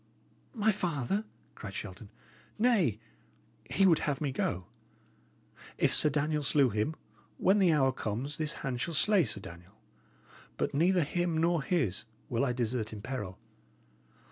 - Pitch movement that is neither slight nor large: No, wide, 6.7 semitones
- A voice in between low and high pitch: Yes, medium, 145 Hz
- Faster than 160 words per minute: No, average, 145 wpm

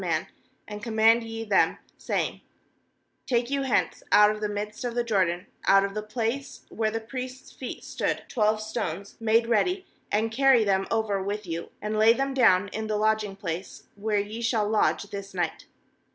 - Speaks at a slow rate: No, average, 180 wpm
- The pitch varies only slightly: Yes, narrow, 2.2 semitones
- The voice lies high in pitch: Yes, high, 215 Hz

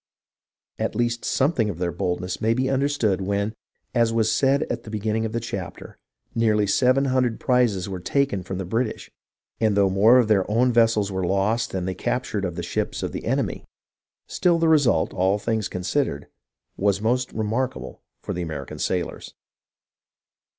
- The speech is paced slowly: No, average, 170 wpm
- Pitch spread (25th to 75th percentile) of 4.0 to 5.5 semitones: Yes, average, 4.5 semitones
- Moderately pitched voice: No, low, 110 Hz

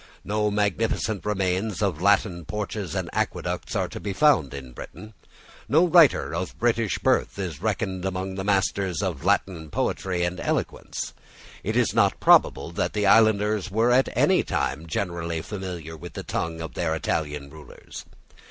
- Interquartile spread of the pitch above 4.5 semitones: No, average, 4.1 semitones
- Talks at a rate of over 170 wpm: No, average, 160 wpm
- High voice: No, very low, 95 Hz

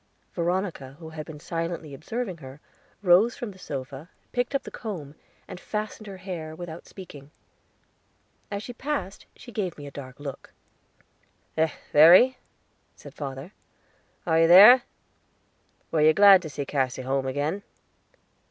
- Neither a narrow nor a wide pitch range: No, wide, 5.7 semitones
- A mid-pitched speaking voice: Yes, medium, 165 Hz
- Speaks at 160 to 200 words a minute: No, average, 145 wpm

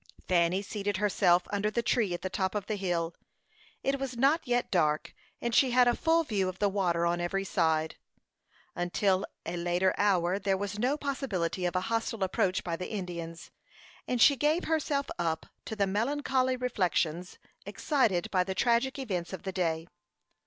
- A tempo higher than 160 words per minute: Yes, average, 180 wpm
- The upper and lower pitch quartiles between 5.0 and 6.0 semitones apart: Yes, wide, 5.6 semitones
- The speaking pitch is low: No, high, 195 Hz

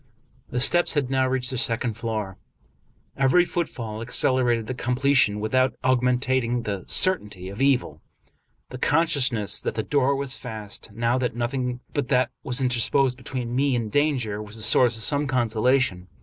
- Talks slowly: No, average, 165 wpm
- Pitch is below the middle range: Yes, low, 125 Hz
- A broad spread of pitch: No, average, 2.8 semitones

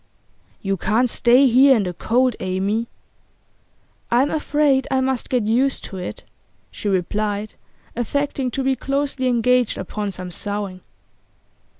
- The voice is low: No, high, 240 Hz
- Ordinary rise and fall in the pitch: Yes, average, 4.5 semitones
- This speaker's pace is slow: Yes, slow, 130 wpm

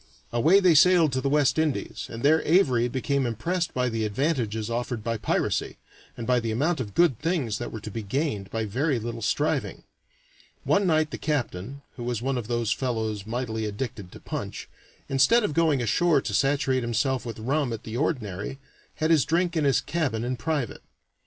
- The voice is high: No, low, 130 Hz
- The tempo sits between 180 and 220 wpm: Yes, average, 190 wpm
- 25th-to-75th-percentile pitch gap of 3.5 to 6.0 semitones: Yes, average, 5.1 semitones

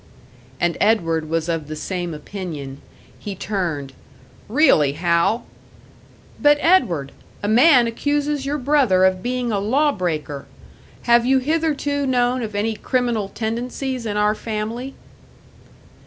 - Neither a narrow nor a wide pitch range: No, wide, 7.0 semitones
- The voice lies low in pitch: No, high, 220 Hz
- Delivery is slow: Yes, slow, 130 wpm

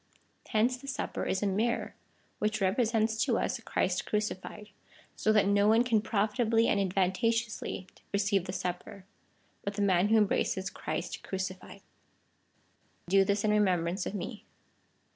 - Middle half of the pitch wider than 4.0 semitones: No, narrow, 2.5 semitones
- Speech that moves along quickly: No, average, 145 wpm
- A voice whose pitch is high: Yes, high, 205 Hz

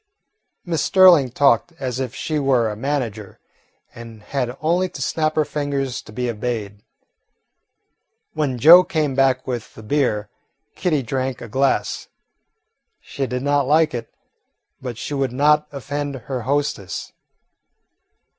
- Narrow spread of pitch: No, average, 3.4 semitones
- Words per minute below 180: Yes, slow, 135 wpm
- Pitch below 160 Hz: Yes, low, 135 Hz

